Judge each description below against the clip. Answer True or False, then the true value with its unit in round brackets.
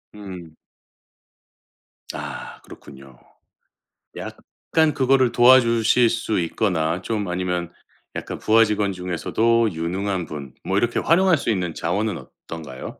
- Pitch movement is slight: False (5.3 semitones)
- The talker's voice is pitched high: False (100 Hz)